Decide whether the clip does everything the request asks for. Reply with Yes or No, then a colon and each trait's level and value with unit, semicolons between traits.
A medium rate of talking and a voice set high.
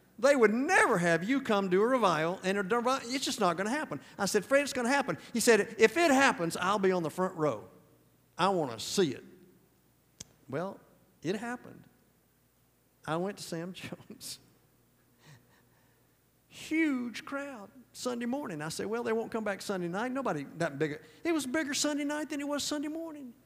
Yes: average, 190 wpm; high, 230 Hz